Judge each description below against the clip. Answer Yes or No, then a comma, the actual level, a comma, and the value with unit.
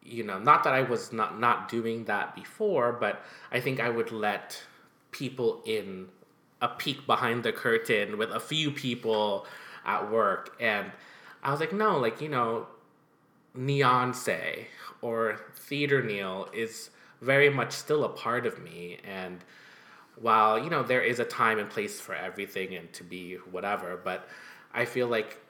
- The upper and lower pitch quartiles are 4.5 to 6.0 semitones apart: Yes, average, 4.9 semitones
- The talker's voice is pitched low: Yes, low, 120 Hz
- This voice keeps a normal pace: Yes, average, 165 wpm